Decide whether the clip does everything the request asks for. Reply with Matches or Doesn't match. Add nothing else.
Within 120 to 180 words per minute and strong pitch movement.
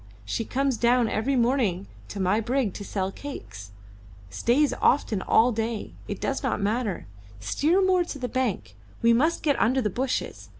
Doesn't match